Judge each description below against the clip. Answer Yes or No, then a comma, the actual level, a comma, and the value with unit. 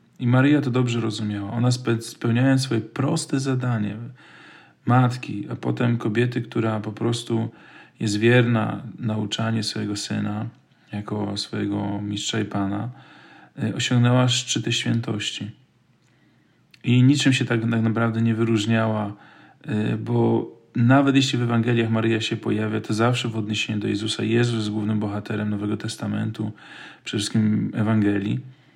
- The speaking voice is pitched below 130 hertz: Yes, low, 115 Hz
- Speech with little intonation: Yes, narrow, 2.3 semitones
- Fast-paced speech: No, average, 125 wpm